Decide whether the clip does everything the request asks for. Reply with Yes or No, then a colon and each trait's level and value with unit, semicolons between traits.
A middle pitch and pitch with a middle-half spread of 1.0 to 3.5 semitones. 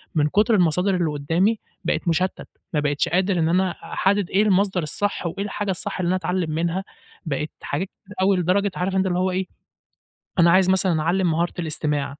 Yes: medium, 180 Hz; average, 2.7 semitones